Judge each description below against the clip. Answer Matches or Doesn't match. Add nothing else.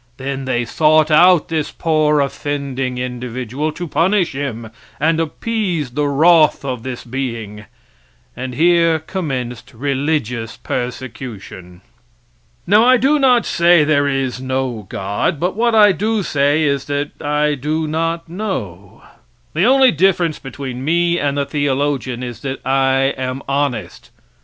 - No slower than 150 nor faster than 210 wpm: Doesn't match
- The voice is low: Doesn't match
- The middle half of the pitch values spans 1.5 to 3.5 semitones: Doesn't match